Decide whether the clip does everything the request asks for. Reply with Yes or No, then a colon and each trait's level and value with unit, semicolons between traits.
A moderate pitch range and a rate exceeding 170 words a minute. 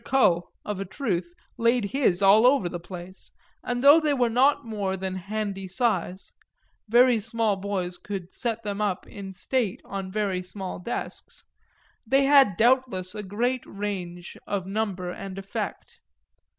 No: average, 4.2 semitones; average, 155 wpm